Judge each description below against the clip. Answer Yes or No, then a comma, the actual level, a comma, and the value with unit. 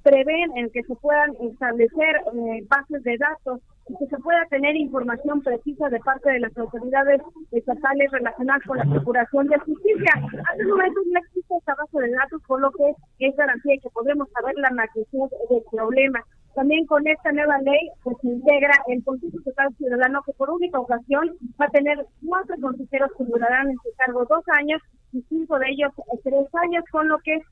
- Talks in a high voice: Yes, very high, 275 Hz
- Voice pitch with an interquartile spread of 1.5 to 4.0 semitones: Yes, average, 3.1 semitones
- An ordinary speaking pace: No, fast, 195 wpm